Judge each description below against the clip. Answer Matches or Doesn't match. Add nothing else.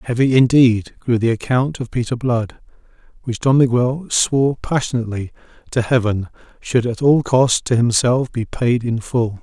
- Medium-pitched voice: Doesn't match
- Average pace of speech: Matches